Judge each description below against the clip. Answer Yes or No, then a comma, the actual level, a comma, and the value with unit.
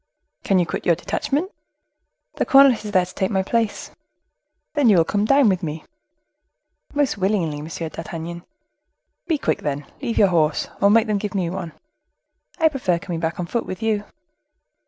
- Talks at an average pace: Yes, average, 180 wpm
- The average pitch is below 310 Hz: Yes, high, 190 Hz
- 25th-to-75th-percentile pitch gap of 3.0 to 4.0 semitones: No, average, 4.9 semitones